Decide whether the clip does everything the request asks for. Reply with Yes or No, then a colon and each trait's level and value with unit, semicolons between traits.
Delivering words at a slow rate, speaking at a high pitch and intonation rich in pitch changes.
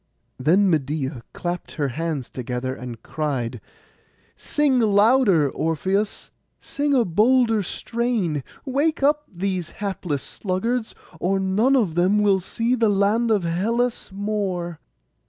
Yes: slow, 120 wpm; high, 195 Hz; wide, 6.1 semitones